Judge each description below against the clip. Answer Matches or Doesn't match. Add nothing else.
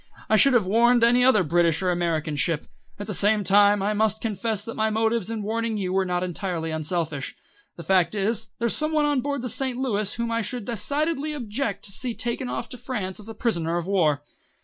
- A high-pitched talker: Matches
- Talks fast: Matches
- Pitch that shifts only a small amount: Doesn't match